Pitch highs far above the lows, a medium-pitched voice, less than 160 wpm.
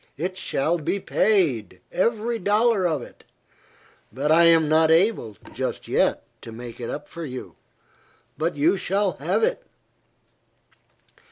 Yes: wide, 5.7 semitones; medium, 170 Hz; average, 140 wpm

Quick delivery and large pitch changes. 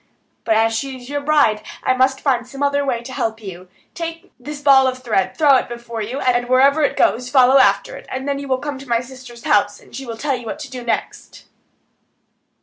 No: fast, 230 wpm; average, 2.9 semitones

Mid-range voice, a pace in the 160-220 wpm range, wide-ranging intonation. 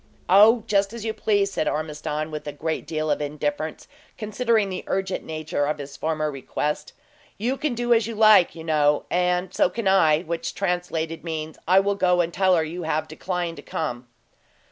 No: medium, 170 Hz; average, 190 wpm; average, 4.3 semitones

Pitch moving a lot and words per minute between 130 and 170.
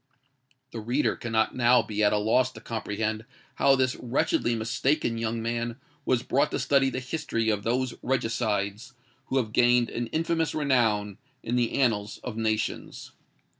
No: average, 2.8 semitones; average, 160 wpm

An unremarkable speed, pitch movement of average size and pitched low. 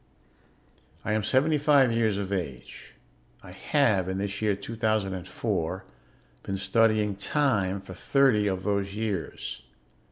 No: slow, 125 wpm; average, 3.0 semitones; low, 100 Hz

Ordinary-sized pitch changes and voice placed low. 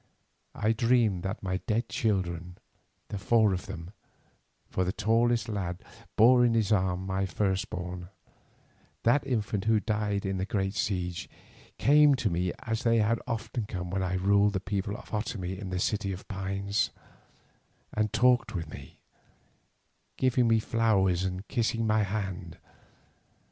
Yes: average, 3.3 semitones; low, 100 Hz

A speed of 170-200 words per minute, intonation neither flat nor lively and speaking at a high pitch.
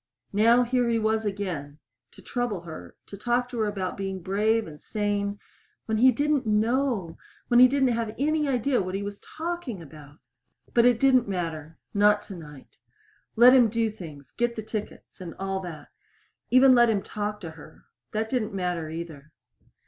Yes: average, 175 wpm; average, 4.9 semitones; high, 210 Hz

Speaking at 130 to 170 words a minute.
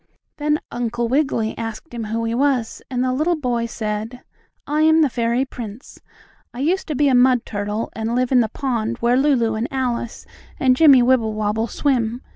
No: average, 185 wpm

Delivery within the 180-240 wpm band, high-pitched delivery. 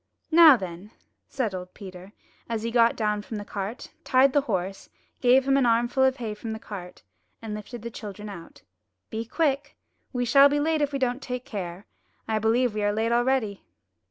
Yes: average, 195 wpm; high, 230 Hz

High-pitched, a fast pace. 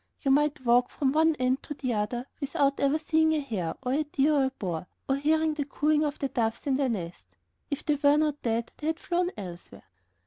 Yes: very high, 275 Hz; fast, 230 wpm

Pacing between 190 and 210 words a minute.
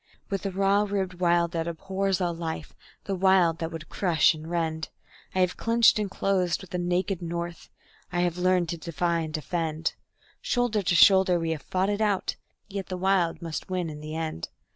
Yes: average, 195 wpm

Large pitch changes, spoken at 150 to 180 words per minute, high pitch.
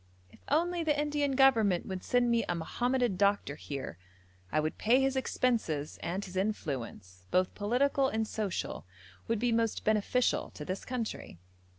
Yes: wide, 6.0 semitones; average, 160 wpm; high, 220 Hz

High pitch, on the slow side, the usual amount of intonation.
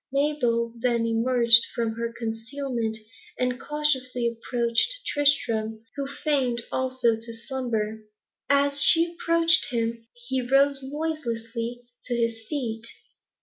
Yes: high, 245 Hz; slow, 110 wpm; average, 3.4 semitones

